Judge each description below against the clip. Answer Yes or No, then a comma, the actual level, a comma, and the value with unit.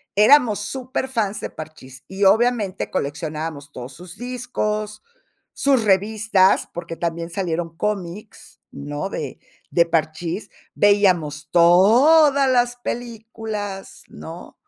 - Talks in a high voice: Yes, high, 195 Hz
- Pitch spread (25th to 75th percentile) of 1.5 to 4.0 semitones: No, average, 5.1 semitones